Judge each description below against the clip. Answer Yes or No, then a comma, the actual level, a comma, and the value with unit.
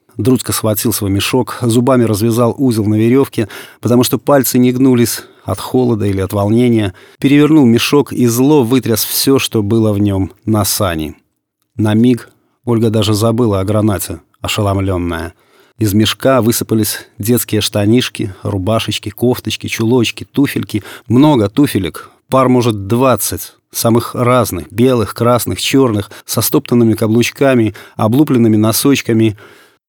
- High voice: No, low, 115 Hz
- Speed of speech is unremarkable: Yes, average, 125 wpm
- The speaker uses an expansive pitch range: No, average, 2.9 semitones